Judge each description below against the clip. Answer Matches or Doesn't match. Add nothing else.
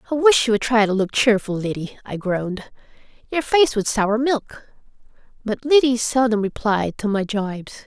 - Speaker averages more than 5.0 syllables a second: Doesn't match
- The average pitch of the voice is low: Doesn't match